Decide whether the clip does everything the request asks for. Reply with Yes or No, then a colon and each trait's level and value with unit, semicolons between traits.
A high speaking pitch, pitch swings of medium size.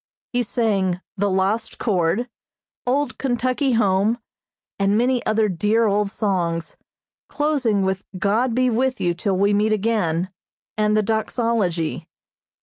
Yes: high, 215 Hz; average, 3.5 semitones